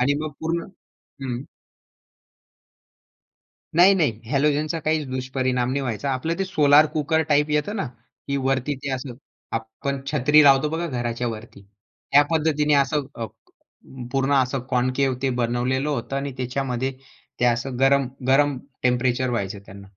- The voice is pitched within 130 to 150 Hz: Yes, low, 135 Hz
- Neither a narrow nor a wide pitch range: Yes, average, 3.0 semitones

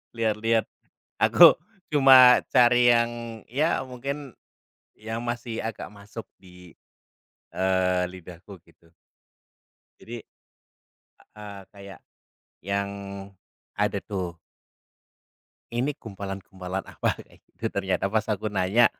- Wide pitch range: No, average, 4.1 semitones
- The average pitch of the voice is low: Yes, low, 105 Hz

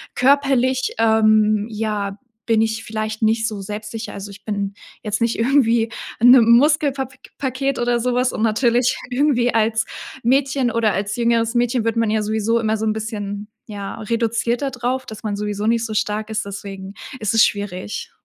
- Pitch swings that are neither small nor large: No, narrow, 2.2 semitones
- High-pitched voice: Yes, high, 225 Hz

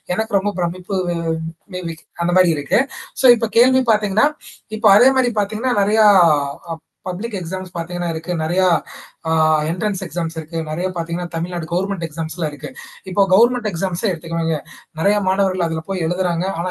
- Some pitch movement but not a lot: Yes, average, 3.6 semitones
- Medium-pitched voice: Yes, medium, 180 Hz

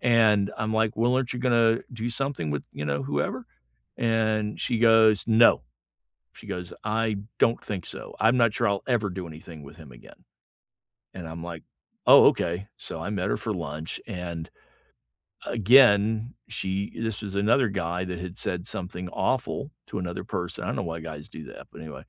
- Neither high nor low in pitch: No, low, 100 Hz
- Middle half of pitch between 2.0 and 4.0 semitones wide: No, average, 4.6 semitones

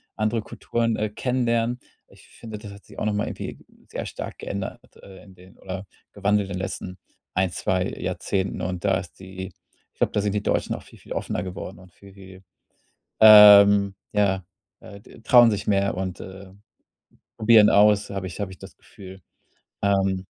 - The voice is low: Yes, low, 100 Hz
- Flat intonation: Yes, narrow, 1.9 semitones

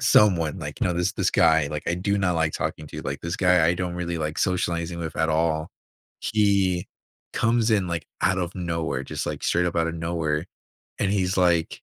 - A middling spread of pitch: No, narrow, 2.2 semitones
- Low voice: Yes, very low, 85 Hz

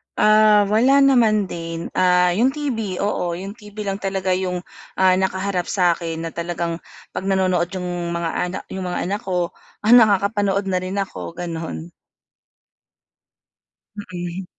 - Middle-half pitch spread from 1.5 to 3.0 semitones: Yes, narrow, 2.6 semitones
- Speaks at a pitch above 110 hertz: Yes, medium, 185 Hz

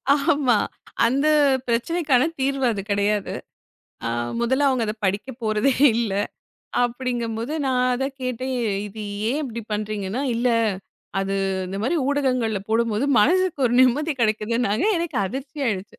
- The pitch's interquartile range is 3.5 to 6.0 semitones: Yes, average, 4.2 semitones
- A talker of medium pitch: No, high, 245 Hz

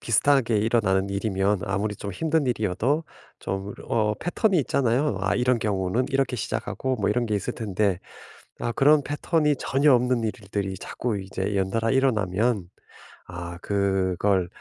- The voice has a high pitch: No, low, 110 Hz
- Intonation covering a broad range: No, average, 4.6 semitones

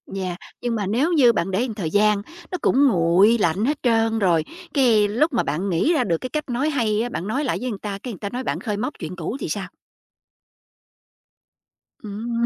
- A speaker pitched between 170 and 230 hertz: Yes, high, 220 Hz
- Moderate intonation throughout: Yes, average, 4.4 semitones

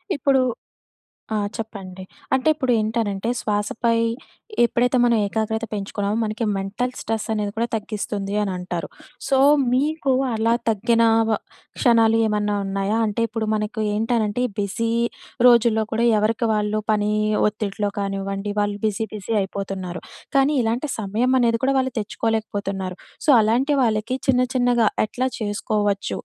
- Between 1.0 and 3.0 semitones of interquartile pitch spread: Yes, narrow, 2.4 semitones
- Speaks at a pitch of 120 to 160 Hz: No, high, 220 Hz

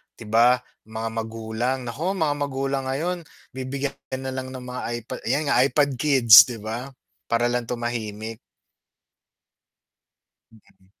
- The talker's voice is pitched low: Yes, low, 125 Hz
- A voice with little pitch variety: No, average, 3.1 semitones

